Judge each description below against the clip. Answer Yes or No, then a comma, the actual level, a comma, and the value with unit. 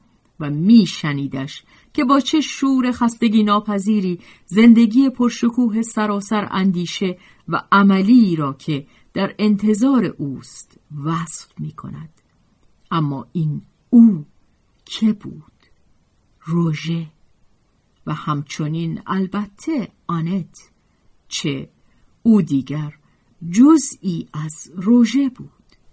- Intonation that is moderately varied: No, wide, 6.7 semitones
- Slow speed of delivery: Yes, slow, 90 wpm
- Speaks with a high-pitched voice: Yes, high, 195 Hz